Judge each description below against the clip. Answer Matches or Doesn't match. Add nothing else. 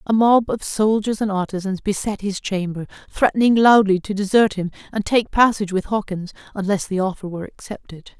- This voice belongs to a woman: Matches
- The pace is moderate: Matches